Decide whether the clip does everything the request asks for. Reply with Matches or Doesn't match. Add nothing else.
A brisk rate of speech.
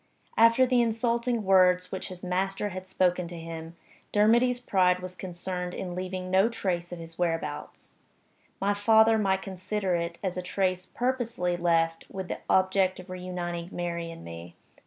Doesn't match